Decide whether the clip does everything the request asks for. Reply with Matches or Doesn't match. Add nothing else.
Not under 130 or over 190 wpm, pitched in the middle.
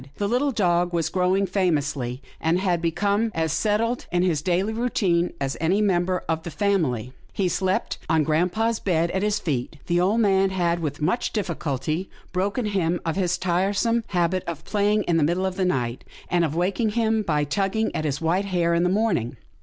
Doesn't match